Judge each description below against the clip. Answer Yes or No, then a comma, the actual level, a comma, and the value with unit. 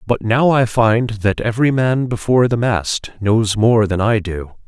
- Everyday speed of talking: Yes, average, 190 wpm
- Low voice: Yes, low, 110 Hz